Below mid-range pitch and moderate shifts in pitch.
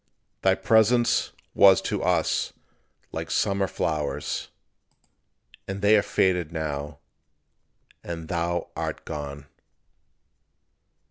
Yes: very low, 85 Hz; average, 4.1 semitones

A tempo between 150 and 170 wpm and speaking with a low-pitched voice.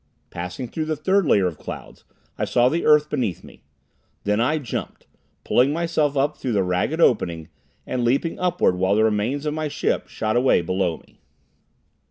No: average, 180 wpm; low, 125 Hz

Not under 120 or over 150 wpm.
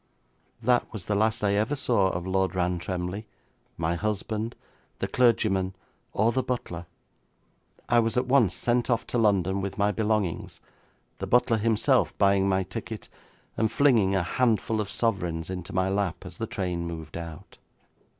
No: average, 160 wpm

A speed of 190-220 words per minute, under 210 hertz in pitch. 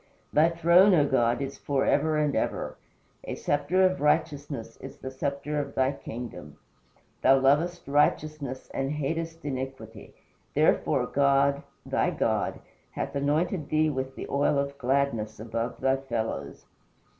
No: average, 140 wpm; medium, 140 Hz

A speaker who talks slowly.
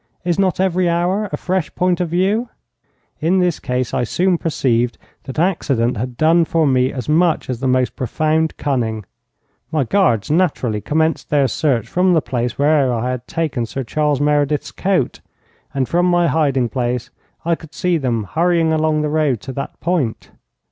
No: average, 175 wpm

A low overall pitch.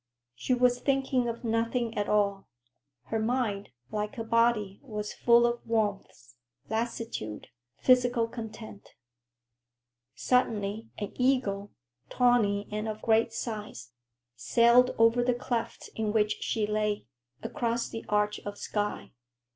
No: high, 225 Hz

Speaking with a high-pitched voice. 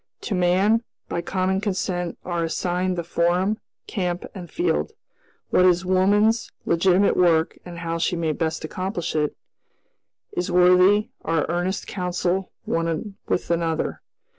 No: medium, 180 Hz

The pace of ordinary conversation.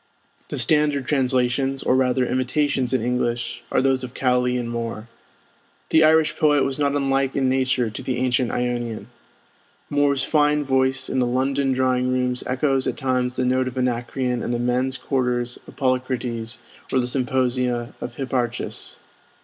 Yes: average, 160 wpm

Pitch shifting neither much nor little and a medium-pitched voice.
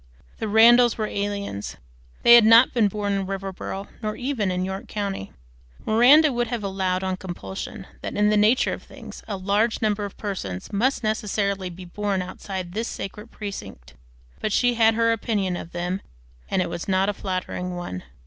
No: average, 3.0 semitones; high, 200 Hz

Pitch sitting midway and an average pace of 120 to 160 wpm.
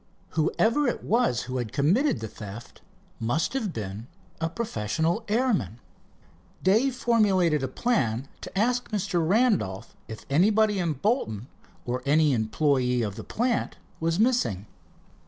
Yes: medium, 165 Hz; slow, 135 wpm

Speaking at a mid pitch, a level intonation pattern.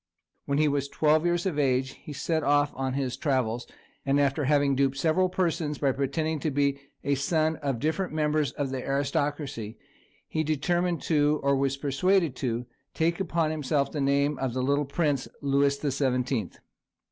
Yes: medium, 145 Hz; narrow, 2.3 semitones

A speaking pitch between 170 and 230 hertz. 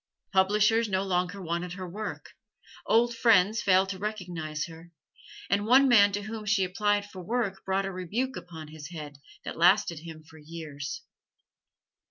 Yes: high, 190 Hz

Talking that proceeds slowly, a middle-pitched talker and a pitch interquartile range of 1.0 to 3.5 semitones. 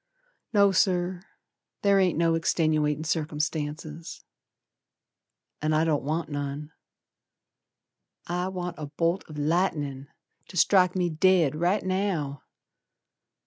Yes: slow, 105 wpm; medium, 165 Hz; average, 3.2 semitones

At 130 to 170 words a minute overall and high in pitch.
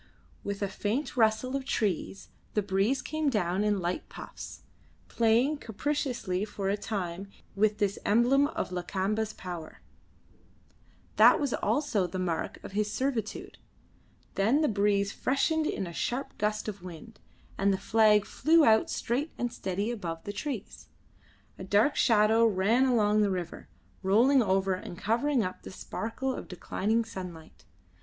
Yes: average, 150 wpm; high, 210 Hz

